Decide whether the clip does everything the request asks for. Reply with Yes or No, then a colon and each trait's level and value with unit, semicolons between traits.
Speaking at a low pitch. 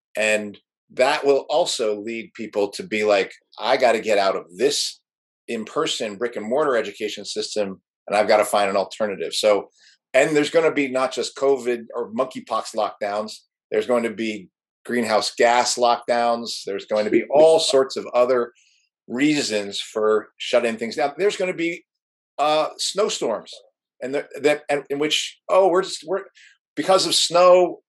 Yes: low, 130 Hz